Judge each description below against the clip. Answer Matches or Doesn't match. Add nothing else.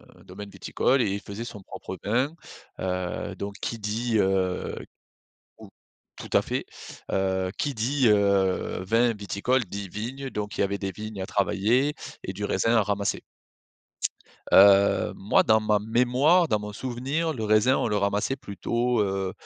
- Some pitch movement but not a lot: Matches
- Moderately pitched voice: Doesn't match